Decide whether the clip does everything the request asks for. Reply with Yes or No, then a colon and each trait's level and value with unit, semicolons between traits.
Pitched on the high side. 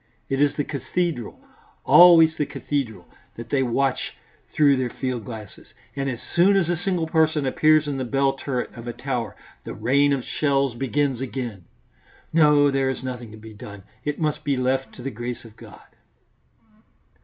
No: low, 135 Hz